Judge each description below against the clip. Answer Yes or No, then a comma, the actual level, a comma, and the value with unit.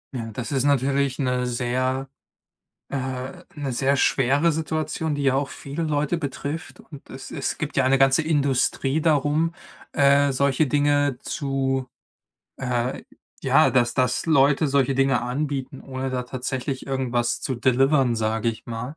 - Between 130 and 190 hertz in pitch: Yes, low, 135 Hz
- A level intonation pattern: Yes, narrow, 2.0 semitones